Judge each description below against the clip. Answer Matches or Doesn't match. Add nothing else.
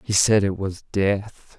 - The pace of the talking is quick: Doesn't match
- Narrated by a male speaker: Matches